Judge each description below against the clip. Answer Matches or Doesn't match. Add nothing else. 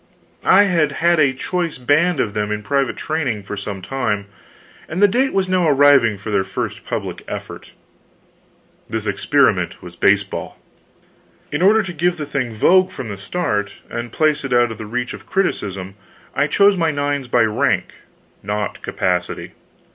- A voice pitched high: Doesn't match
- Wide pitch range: Matches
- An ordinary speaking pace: Matches